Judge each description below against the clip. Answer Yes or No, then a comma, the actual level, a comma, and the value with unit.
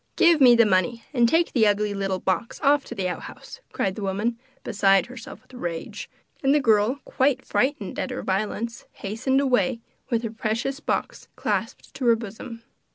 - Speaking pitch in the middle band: No, high, 230 Hz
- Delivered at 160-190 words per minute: Yes, average, 180 wpm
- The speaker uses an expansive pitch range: No, average, 4.2 semitones